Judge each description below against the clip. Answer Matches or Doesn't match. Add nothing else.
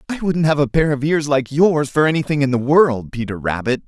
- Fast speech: Matches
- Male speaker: Matches